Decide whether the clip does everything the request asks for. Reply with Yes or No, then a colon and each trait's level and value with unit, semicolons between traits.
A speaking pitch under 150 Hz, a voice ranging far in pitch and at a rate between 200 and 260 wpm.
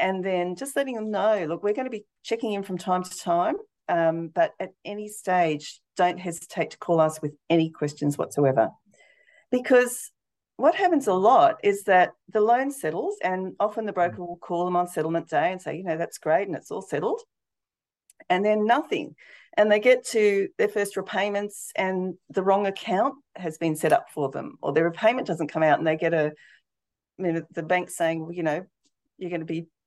No: high, 190 Hz; wide, 6.4 semitones; fast, 205 wpm